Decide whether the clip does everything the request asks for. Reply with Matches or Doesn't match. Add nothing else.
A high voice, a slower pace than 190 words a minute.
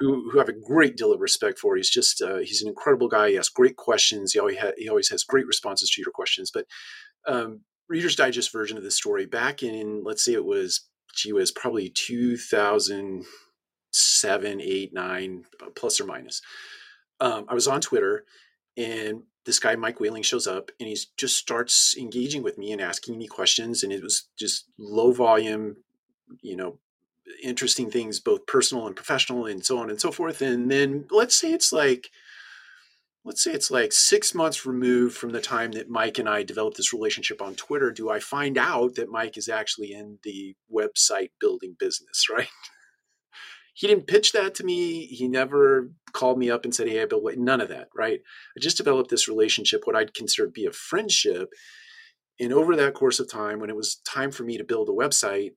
Doesn't match